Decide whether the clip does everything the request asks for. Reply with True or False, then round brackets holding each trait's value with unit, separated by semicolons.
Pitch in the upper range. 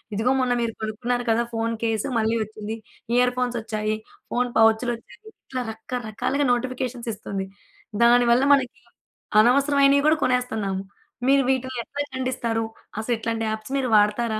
True (240 Hz)